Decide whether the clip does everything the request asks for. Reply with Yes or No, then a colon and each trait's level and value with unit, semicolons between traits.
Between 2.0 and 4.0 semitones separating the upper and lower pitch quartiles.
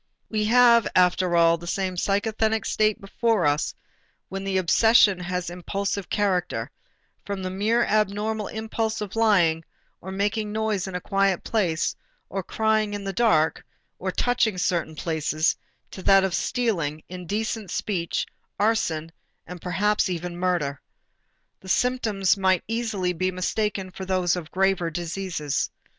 Yes: average, 3.3 semitones